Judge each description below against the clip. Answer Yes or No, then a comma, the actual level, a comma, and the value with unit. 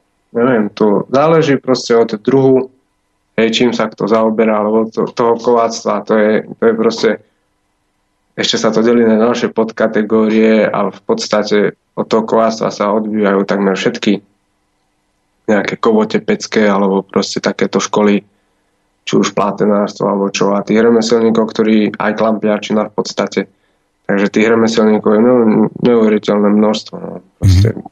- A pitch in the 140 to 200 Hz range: No, low, 110 Hz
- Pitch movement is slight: Yes, narrow, 2.2 semitones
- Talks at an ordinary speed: Yes, average, 140 wpm